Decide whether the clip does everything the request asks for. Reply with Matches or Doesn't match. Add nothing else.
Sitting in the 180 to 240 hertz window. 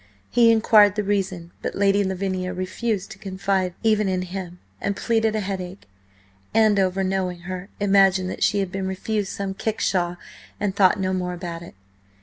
Matches